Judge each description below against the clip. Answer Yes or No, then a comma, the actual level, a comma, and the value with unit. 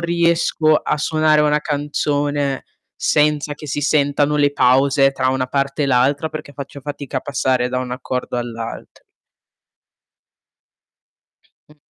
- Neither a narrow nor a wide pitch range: No, narrow, 2.2 semitones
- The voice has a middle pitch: Yes, medium, 145 Hz